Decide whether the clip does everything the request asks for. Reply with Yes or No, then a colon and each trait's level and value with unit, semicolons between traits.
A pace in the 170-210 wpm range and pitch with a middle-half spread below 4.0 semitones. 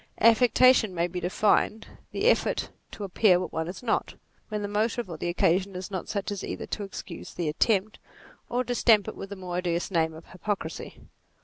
Yes: average, 200 wpm; average, 3.5 semitones